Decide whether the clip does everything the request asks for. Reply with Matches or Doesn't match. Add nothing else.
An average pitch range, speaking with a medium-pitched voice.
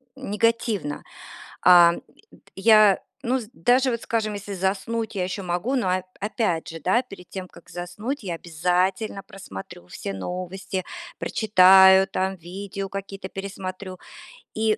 Doesn't match